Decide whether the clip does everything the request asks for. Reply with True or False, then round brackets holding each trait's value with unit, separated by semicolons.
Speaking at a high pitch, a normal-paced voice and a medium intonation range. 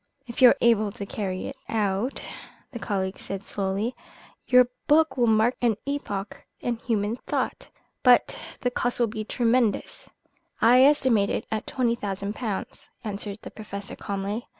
True (220 Hz; 155 wpm; 3.5 semitones)